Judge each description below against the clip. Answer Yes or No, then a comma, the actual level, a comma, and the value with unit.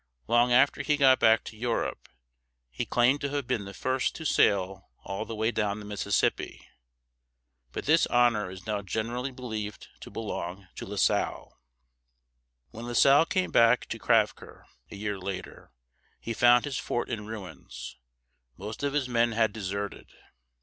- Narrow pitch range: No, average, 3.5 semitones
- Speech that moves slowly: No, average, 165 wpm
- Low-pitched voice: Yes, low, 115 Hz